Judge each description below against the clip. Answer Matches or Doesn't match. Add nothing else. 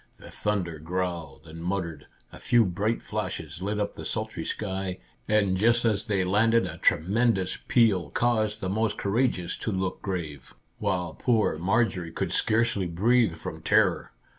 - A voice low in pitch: Matches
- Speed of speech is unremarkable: Matches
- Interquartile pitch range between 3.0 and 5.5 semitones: Matches